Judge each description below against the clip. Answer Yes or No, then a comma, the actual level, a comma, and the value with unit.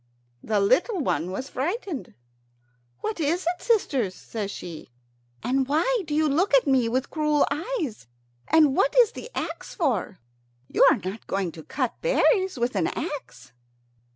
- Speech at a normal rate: Yes, average, 155 wpm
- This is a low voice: No, very high, 280 Hz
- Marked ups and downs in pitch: Yes, wide, 7.8 semitones